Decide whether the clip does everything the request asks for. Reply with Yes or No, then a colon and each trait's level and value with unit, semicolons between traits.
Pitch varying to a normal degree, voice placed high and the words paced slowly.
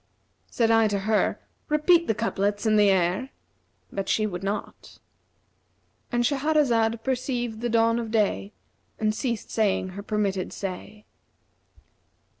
Yes: average, 3.0 semitones; high, 220 Hz; slow, 125 wpm